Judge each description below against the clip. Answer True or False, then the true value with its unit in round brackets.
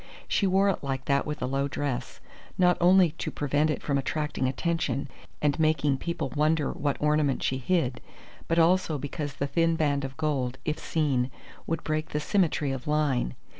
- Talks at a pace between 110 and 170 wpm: False (180 wpm)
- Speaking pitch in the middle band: True (150 Hz)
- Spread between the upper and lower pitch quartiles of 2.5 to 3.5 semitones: True (2.9 semitones)